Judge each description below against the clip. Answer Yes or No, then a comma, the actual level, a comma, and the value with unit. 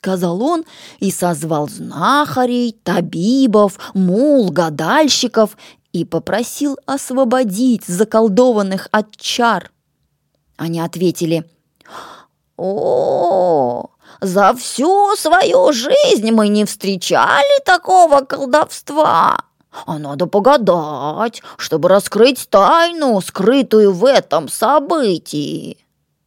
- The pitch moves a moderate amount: No, wide, 7.2 semitones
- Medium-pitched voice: No, high, 220 Hz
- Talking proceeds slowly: Yes, slow, 80 wpm